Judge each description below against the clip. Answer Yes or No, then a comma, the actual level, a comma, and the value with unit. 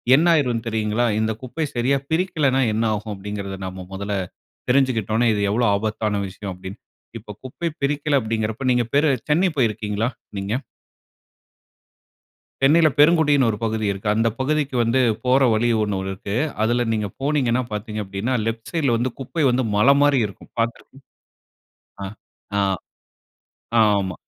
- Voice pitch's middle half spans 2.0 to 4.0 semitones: No, average, 4.5 semitones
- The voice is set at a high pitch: No, low, 115 Hz